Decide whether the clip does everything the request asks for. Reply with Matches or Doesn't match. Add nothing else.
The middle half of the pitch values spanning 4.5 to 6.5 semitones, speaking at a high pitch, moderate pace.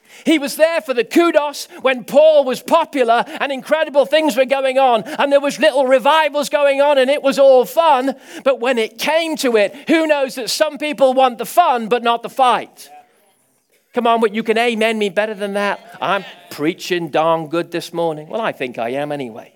Doesn't match